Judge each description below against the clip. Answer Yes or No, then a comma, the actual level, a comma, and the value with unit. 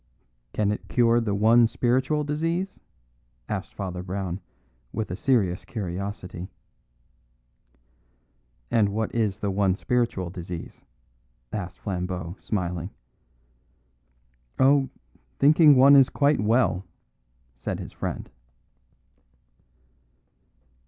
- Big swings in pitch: Yes, wide, 5.8 semitones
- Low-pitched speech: Yes, low, 105 Hz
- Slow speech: Yes, slow, 95 wpm